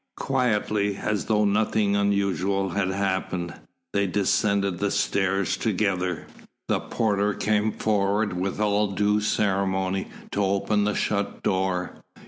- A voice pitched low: Yes, low, 100 Hz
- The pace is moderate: No, slow, 120 wpm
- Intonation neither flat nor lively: No, narrow, 1.5 semitones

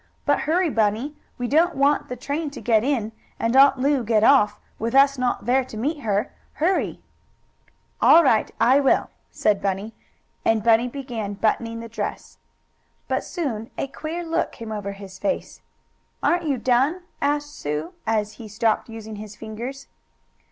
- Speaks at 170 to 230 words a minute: No, average, 160 wpm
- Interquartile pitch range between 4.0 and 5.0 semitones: Yes, average, 4.7 semitones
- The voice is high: Yes, high, 245 Hz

